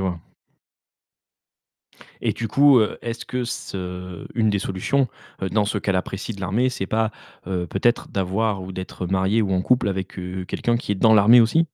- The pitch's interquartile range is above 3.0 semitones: Yes, average, 3.5 semitones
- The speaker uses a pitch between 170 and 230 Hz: No, low, 100 Hz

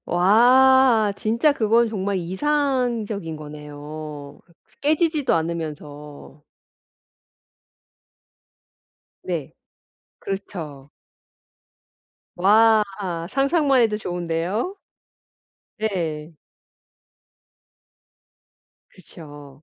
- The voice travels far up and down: Yes, wide, 7.3 semitones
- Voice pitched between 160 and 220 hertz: Yes, high, 190 Hz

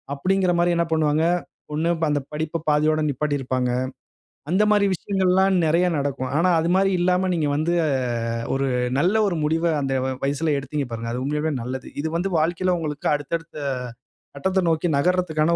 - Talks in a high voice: No, medium, 155 Hz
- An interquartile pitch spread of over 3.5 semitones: Yes, average, 3.9 semitones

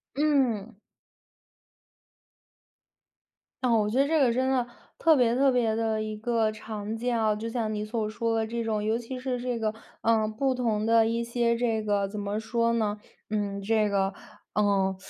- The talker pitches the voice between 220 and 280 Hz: Yes, high, 225 Hz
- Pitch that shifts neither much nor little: No, narrow, 2.1 semitones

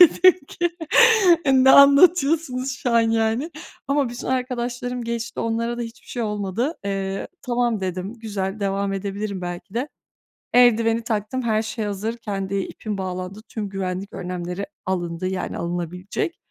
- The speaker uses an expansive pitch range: No, average, 4.1 semitones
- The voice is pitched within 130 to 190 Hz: No, high, 220 Hz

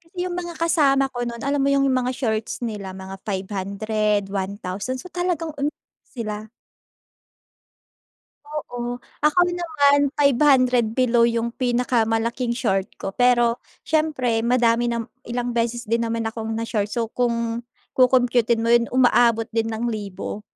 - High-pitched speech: Yes, high, 235 Hz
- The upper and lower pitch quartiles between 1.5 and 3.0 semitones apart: Yes, narrow, 2.6 semitones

